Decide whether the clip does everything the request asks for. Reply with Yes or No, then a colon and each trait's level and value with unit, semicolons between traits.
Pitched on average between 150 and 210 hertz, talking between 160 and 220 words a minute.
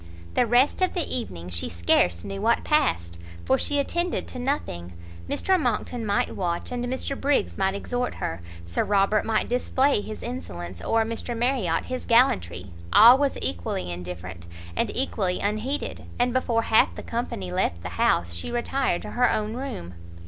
No: high, 220 Hz; average, 170 wpm